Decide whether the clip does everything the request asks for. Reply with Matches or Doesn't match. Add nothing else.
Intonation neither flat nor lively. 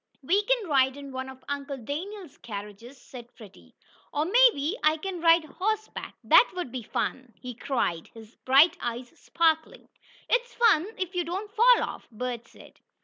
Doesn't match